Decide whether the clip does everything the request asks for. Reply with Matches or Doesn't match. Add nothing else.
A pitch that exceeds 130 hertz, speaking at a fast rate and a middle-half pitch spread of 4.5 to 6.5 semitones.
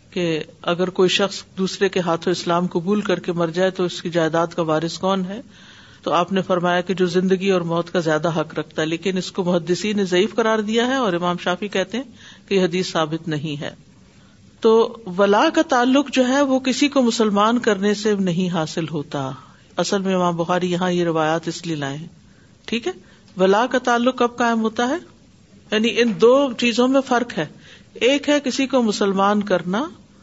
Matches